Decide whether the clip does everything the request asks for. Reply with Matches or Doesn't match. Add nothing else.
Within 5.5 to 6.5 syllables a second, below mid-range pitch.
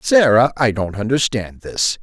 Doesn't match